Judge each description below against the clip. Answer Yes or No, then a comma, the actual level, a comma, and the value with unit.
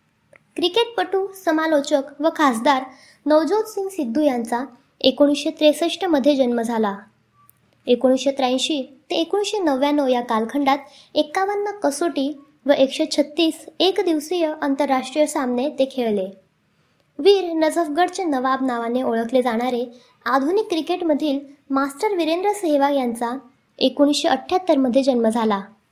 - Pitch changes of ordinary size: Yes, average, 4.0 semitones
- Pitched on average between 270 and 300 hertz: Yes, very high, 285 Hz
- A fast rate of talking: No, average, 115 wpm